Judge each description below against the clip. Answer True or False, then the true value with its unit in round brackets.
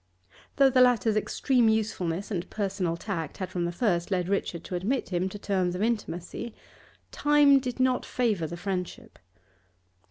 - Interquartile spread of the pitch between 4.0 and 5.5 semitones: True (5.0 semitones)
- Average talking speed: True (160 wpm)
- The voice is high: True (200 Hz)